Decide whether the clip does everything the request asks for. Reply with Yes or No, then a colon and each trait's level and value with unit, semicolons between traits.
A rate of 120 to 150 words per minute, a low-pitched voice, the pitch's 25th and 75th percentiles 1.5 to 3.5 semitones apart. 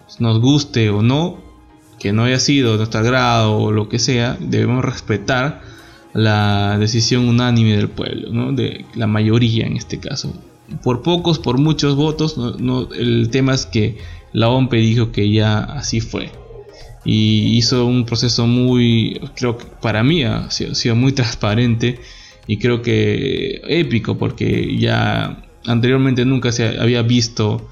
No: average, 160 wpm; low, 120 Hz; average, 2.8 semitones